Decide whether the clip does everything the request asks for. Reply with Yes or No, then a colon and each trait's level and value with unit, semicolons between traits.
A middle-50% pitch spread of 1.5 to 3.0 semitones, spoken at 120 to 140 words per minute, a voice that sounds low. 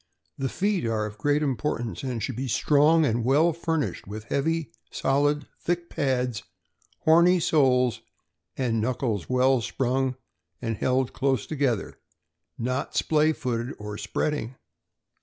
No: average, 3.9 semitones; slow, 135 wpm; low, 130 Hz